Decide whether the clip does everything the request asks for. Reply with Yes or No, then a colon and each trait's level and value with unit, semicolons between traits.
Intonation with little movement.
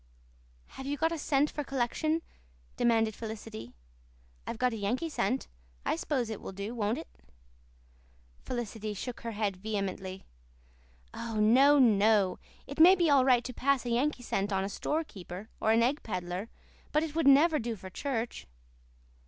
No: average, 5.0 semitones